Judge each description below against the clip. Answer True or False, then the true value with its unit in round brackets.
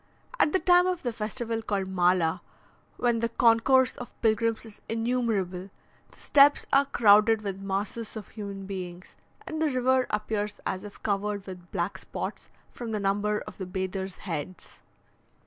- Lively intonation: False (3.5 semitones)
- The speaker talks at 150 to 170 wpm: True (160 wpm)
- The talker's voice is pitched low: False (210 Hz)